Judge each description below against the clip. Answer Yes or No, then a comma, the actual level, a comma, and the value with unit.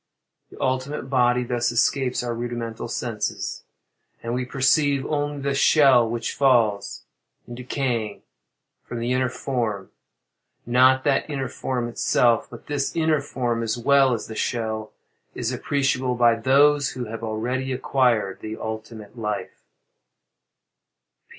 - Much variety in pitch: No, narrow, 2.6 semitones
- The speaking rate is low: Yes, slow, 130 wpm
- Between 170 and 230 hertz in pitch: No, low, 125 Hz